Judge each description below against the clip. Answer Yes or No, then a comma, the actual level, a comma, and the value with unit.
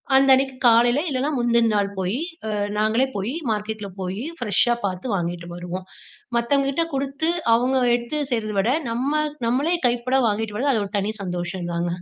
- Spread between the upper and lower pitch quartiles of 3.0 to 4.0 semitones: No, average, 4.9 semitones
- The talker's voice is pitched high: Yes, high, 230 Hz